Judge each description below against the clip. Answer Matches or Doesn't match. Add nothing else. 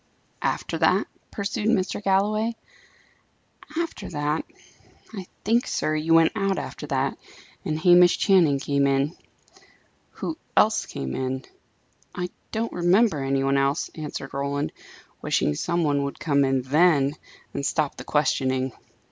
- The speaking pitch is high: Doesn't match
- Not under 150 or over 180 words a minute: Doesn't match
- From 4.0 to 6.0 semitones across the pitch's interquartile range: Matches